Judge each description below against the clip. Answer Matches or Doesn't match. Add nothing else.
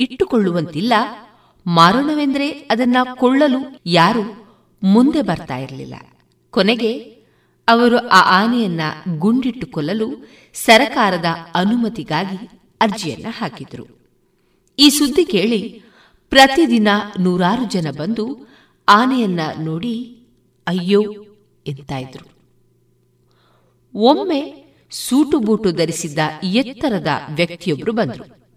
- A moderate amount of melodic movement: Doesn't match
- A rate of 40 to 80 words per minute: Matches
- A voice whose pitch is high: Matches